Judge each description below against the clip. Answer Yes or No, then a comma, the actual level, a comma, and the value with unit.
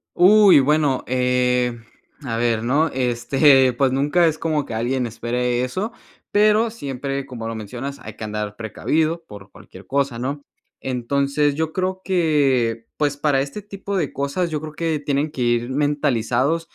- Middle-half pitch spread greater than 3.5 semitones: Yes, average, 4.2 semitones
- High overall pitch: No, medium, 140 Hz